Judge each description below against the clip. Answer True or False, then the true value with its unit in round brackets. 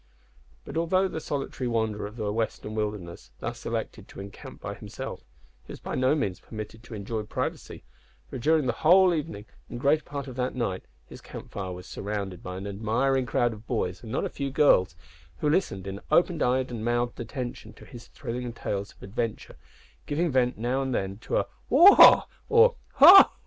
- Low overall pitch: True (120 Hz)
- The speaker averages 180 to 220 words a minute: True (190 wpm)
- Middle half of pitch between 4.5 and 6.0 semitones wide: True (5.1 semitones)